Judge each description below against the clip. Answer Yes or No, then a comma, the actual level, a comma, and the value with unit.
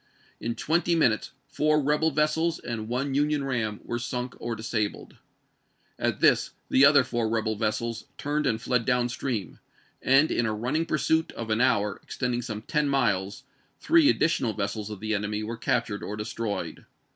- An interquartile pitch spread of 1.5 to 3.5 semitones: No, average, 4.7 semitones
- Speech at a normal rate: Yes, average, 170 wpm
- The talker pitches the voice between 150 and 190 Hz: No, low, 120 Hz